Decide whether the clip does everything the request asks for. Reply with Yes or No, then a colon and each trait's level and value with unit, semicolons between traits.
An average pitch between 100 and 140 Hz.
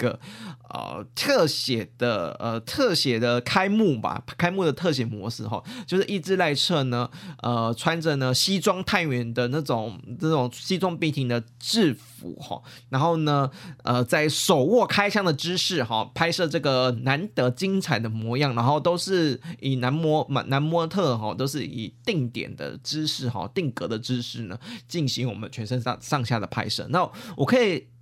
Yes: low, 135 Hz